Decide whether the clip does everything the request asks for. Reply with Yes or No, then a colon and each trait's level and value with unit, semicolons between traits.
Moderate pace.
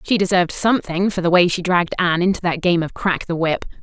No: fast, 250 wpm